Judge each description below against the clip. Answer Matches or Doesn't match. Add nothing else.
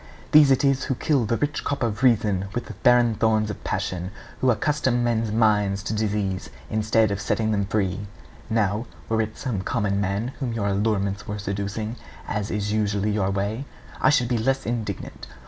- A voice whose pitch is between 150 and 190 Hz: Doesn't match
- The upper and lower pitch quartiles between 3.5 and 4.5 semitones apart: Doesn't match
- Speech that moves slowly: Doesn't match